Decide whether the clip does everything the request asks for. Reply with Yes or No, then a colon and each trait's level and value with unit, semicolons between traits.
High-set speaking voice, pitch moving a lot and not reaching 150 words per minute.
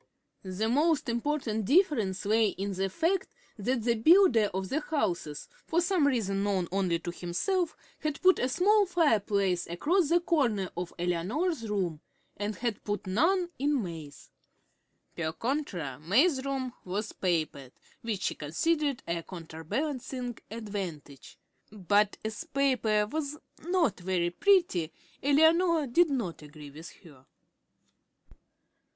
Yes: high, 220 Hz; wide, 8.6 semitones; slow, 135 wpm